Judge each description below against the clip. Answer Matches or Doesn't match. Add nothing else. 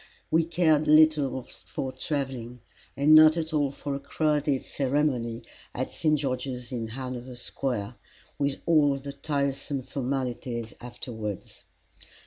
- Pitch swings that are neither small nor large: Matches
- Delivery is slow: Matches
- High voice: Doesn't match